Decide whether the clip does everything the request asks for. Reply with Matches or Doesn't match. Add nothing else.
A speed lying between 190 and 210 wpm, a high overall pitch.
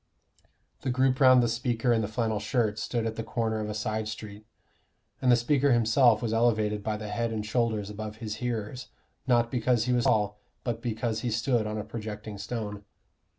Doesn't match